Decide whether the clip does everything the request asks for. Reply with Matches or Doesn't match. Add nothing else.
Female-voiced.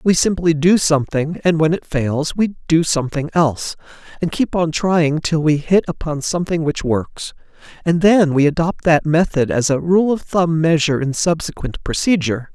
Doesn't match